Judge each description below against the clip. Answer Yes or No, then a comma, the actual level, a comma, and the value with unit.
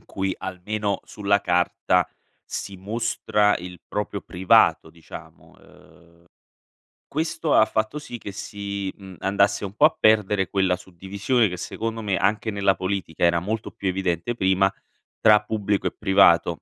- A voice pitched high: No, low, 100 Hz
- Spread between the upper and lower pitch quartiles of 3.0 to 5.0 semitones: No, narrow, 2.4 semitones